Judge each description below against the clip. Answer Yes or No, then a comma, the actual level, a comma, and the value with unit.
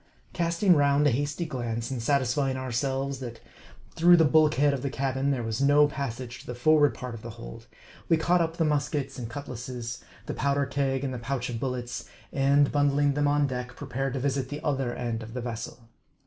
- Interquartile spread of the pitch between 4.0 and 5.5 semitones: No, average, 2.7 semitones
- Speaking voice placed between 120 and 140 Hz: Yes, low, 135 Hz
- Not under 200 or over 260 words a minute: Yes, fast, 205 wpm